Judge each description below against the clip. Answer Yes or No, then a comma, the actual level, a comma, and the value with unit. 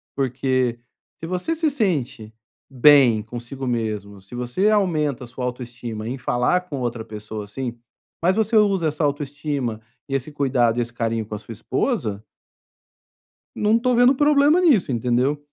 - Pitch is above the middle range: No, low, 130 Hz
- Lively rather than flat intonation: Yes, wide, 7.2 semitones